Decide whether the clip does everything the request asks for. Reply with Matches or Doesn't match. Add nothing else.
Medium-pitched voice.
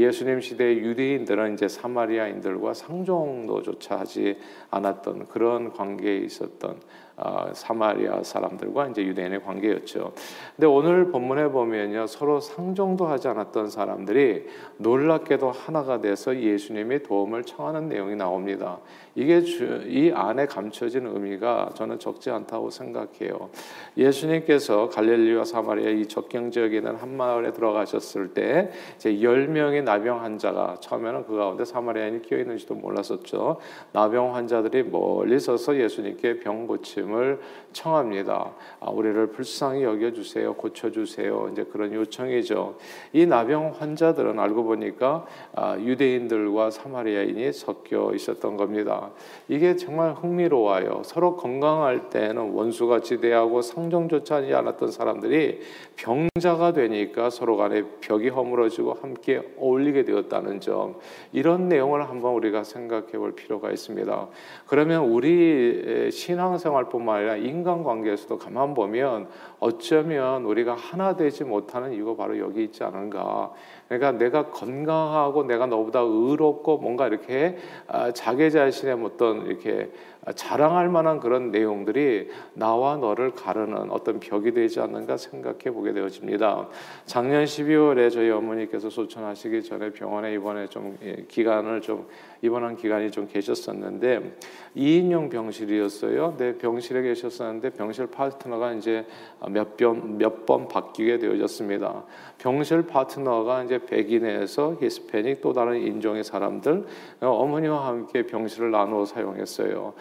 Doesn't match